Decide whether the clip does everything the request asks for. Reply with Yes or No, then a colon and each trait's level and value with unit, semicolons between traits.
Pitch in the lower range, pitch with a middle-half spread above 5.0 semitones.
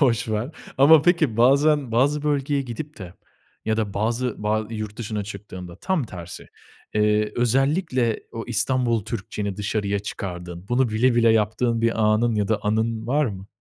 No: low, 115 Hz; average, 3.6 semitones